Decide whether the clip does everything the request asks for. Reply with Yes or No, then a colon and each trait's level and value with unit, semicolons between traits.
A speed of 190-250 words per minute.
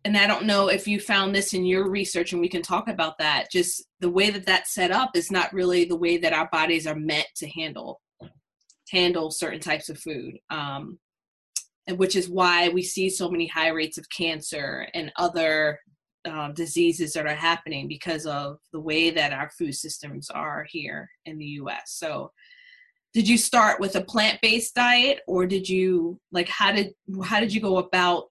Yes: average, 200 wpm